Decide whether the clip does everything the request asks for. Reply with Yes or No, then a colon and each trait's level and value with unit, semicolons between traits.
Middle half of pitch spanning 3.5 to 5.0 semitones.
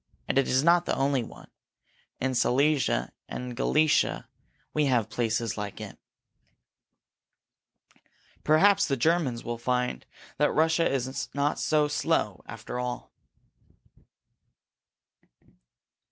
Yes: average, 3.8 semitones